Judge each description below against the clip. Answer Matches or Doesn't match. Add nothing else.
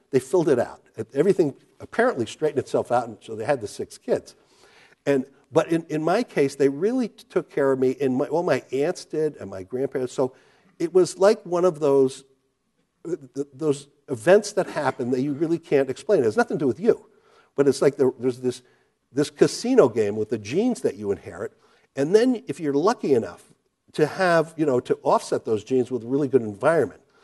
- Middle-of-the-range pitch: Matches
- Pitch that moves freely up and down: Matches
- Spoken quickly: Matches